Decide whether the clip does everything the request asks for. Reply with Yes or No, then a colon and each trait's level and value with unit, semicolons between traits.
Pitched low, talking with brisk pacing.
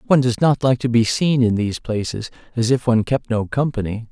Yes: low, 120 Hz; fast, 235 wpm